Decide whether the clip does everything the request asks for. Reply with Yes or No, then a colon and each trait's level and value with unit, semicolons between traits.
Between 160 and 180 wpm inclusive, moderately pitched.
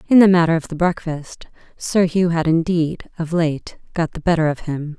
No: fast, 205 wpm; medium, 165 Hz